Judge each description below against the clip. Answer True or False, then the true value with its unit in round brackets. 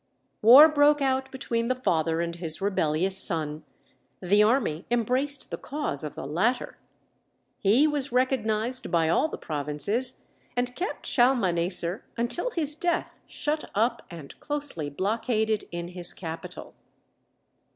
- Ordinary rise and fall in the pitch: False (7.5 semitones)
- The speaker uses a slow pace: True (130 wpm)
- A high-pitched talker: True (220 Hz)